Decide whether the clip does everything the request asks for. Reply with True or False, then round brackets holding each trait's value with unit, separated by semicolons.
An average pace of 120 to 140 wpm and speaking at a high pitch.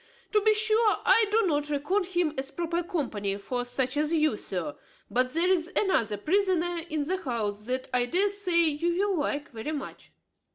False (190 wpm; 315 Hz)